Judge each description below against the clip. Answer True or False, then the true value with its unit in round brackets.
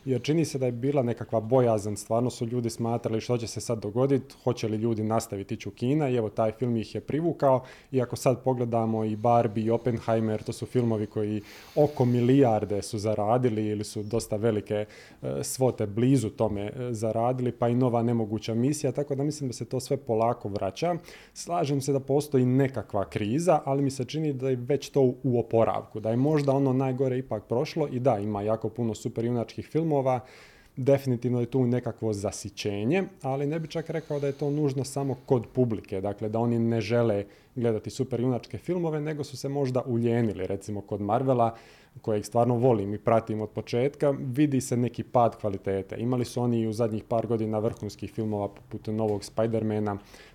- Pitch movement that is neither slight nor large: True (3.3 semitones)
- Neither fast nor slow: False (190 wpm)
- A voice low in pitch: True (120 Hz)